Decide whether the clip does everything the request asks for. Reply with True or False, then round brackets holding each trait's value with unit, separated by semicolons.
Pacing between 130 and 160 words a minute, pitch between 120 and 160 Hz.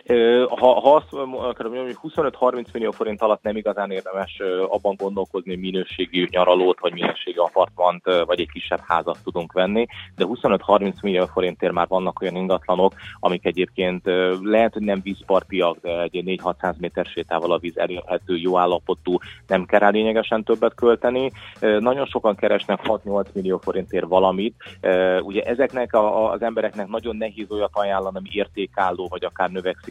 False (150 wpm; 95 Hz)